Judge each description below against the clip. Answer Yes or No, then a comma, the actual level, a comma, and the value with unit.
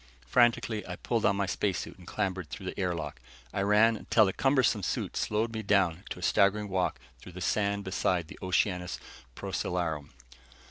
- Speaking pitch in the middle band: No, low, 100 Hz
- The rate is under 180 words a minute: No, average, 185 wpm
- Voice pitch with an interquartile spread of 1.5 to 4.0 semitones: Yes, average, 2.9 semitones